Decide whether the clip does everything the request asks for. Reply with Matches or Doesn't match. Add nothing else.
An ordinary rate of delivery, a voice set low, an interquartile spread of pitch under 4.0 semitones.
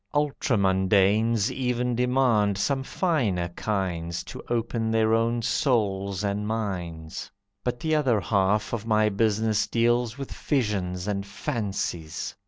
Doesn't match